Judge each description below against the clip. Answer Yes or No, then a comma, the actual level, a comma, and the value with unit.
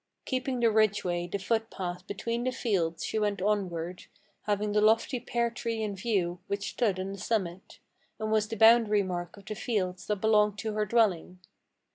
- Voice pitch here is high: Yes, high, 210 Hz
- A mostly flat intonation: No, average, 3.1 semitones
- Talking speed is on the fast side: No, average, 180 wpm